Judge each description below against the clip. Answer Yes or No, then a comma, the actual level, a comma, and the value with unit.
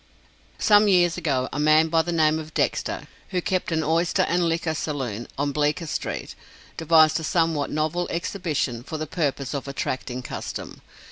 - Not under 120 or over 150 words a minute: No, average, 165 wpm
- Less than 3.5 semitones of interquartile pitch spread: Yes, average, 2.7 semitones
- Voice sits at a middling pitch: Yes, medium, 155 Hz